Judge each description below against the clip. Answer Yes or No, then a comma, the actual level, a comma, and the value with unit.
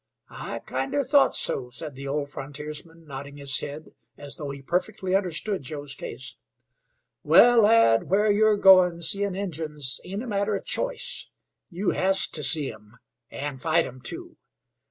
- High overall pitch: No, medium, 160 Hz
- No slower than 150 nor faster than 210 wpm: Yes, average, 155 wpm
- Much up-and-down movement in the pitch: Yes, wide, 6.1 semitones